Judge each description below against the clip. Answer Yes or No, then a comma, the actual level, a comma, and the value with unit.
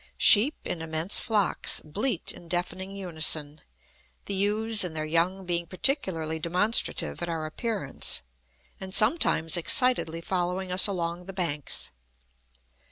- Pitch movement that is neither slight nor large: Yes, average, 3.5 semitones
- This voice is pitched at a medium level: Yes, medium, 180 Hz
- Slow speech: Yes, slow, 125 wpm